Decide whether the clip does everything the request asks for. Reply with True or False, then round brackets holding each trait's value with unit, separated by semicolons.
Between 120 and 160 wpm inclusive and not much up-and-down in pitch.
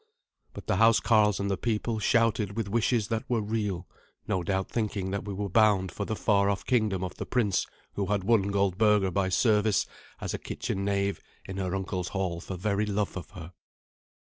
False (195 wpm; 2.1 semitones)